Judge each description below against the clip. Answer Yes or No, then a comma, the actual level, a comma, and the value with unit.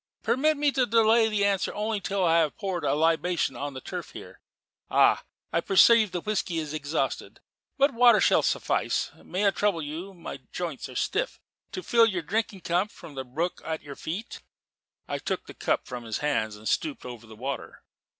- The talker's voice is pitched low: No, medium, 180 Hz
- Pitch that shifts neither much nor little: No, wide, 6.4 semitones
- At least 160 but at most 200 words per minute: Yes, average, 190 wpm